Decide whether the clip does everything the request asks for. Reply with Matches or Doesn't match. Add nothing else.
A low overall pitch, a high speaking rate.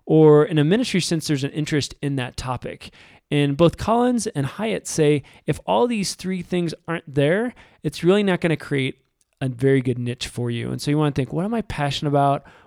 Doesn't match